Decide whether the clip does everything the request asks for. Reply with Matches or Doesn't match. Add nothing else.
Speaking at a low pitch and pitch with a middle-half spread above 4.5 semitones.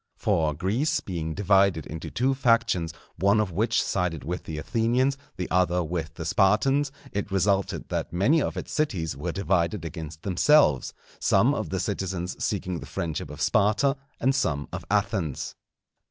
Matches